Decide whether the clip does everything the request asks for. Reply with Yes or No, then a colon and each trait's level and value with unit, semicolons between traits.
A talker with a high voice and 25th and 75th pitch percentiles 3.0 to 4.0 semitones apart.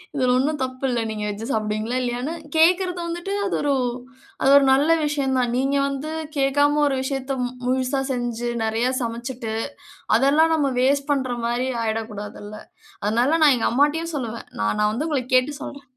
Yes: very high, 265 Hz; average, 3.4 semitones